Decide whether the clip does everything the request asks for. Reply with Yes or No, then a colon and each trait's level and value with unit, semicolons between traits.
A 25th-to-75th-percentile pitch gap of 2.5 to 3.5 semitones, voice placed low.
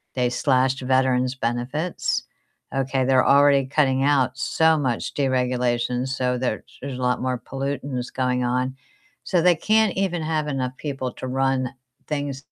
No: narrow, 2.1 semitones; low, 130 Hz